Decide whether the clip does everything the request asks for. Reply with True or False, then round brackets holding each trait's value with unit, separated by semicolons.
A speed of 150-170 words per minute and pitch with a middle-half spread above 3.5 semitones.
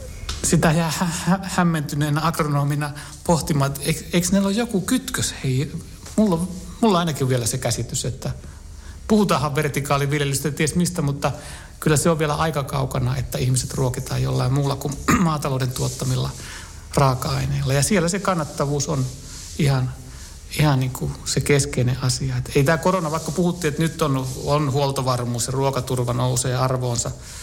True (155 wpm; 4.0 semitones)